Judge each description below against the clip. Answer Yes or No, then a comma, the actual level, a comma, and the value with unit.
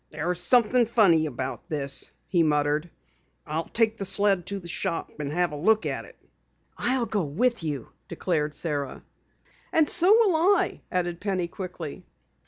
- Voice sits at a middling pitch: Yes, medium, 175 Hz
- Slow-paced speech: No, average, 165 wpm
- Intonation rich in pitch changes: Yes, wide, 6.0 semitones